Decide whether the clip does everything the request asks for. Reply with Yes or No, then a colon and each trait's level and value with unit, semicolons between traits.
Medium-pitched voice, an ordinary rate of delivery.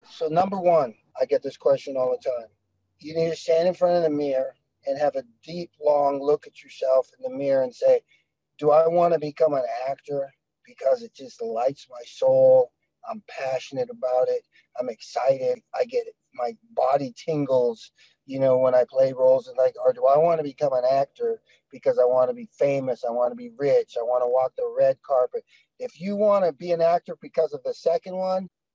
No: medium, 165 Hz; fast, 215 wpm